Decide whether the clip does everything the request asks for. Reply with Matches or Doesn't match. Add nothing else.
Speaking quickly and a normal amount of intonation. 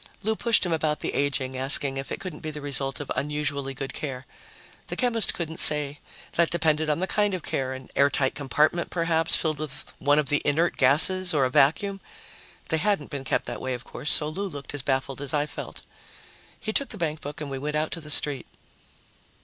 Matches